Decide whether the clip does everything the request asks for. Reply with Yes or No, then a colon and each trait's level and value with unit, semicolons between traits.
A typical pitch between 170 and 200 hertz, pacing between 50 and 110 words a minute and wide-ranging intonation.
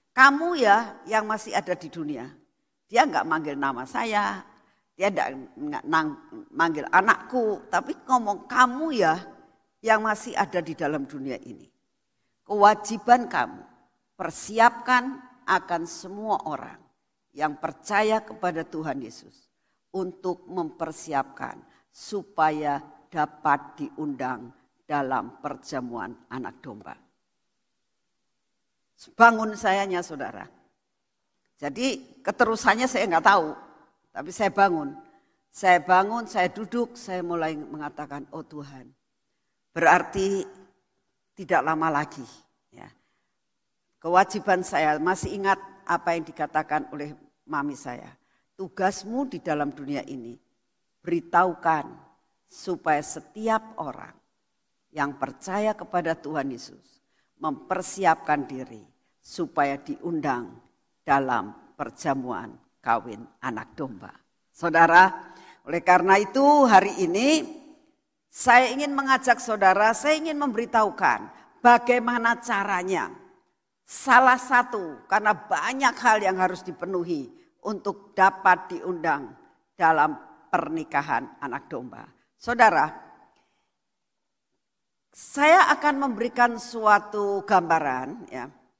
Yes: high, 190 Hz; average, 95 wpm; wide, 6.8 semitones